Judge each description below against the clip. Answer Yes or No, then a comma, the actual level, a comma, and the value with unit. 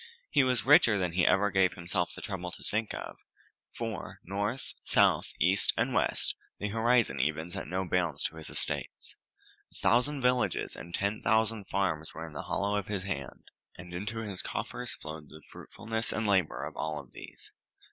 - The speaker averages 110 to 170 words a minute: No, average, 180 wpm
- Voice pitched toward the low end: Yes, very low, 95 Hz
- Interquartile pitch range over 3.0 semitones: Yes, average, 4.5 semitones